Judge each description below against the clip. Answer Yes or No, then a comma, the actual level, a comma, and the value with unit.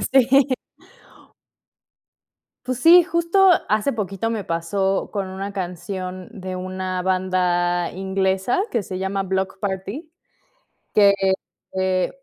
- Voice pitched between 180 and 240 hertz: Yes, high, 190 Hz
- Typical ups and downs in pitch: Yes, average, 3.0 semitones